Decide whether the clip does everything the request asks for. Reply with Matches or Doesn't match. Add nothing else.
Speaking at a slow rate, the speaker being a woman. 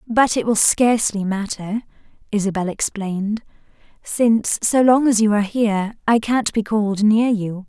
Doesn't match